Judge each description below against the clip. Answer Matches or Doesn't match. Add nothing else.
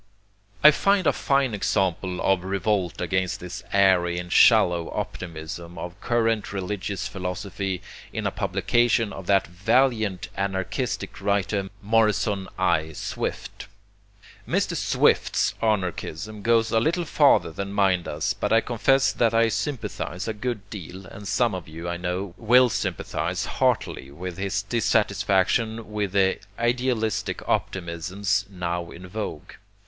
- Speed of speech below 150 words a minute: Matches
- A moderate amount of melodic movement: Matches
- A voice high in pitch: Doesn't match